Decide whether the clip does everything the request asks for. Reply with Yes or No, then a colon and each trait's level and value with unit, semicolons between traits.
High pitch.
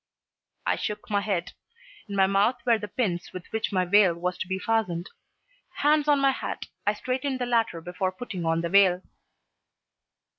Yes: high, 200 Hz